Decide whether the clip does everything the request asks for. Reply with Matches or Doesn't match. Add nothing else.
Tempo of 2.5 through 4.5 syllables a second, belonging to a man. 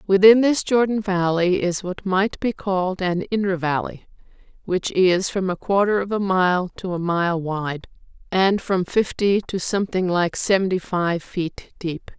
Doesn't match